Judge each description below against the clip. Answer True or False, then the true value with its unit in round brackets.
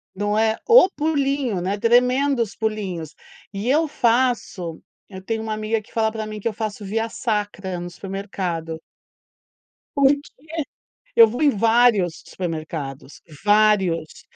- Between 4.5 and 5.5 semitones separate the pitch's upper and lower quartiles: False (3.9 semitones)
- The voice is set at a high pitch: True (215 Hz)